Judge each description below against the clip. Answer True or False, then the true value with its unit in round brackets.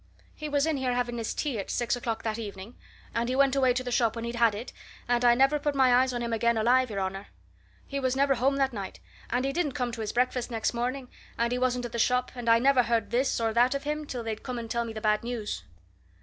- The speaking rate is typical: False (275 wpm)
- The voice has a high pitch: True (245 Hz)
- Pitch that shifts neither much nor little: False (2.1 semitones)